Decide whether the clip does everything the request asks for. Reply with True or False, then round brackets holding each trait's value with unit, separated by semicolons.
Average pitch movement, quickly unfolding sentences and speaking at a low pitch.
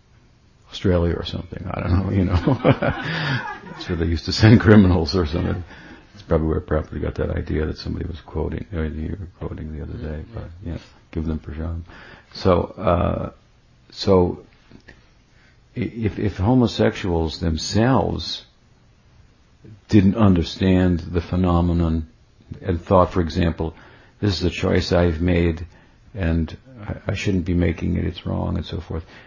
False (3.0 semitones; 150 wpm; 90 Hz)